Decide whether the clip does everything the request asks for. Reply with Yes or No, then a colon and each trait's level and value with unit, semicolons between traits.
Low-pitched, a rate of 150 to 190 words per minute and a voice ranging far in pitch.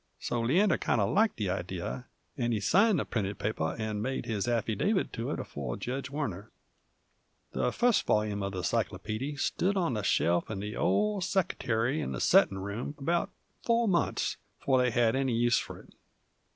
Yes: low, 120 Hz; average, 180 wpm; wide, 6.8 semitones